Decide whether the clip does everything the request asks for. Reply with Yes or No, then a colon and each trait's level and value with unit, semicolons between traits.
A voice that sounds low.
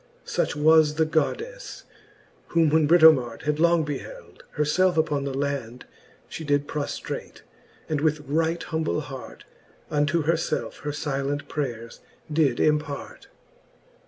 No: medium, 150 Hz